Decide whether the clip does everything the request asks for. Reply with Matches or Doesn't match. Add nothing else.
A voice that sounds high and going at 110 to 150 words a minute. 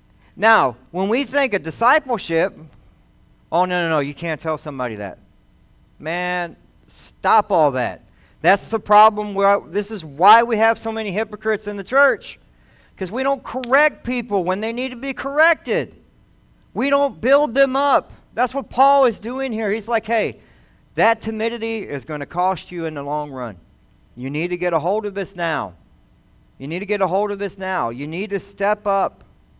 Doesn't match